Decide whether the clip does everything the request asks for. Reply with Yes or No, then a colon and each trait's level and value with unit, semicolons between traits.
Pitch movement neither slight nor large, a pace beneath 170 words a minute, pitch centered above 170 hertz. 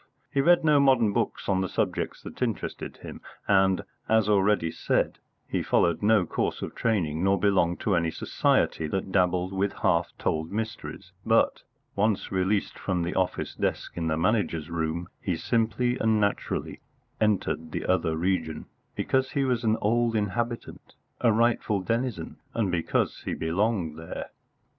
No: average, 4.7 semitones; average, 155 wpm; low, 100 Hz